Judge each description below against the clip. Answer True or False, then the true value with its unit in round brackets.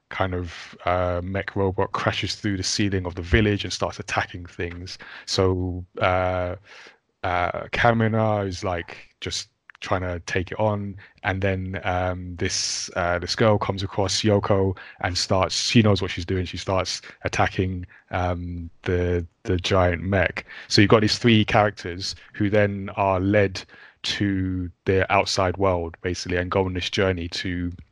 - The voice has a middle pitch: False (95 Hz)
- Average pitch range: False (2.2 semitones)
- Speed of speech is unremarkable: True (160 wpm)